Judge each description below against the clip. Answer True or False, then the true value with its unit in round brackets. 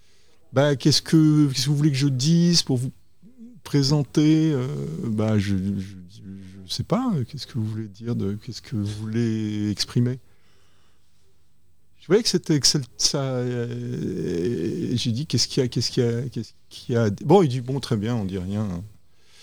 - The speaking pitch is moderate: False (120 Hz)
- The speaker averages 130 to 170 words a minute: False (185 wpm)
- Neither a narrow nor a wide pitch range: False (6.4 semitones)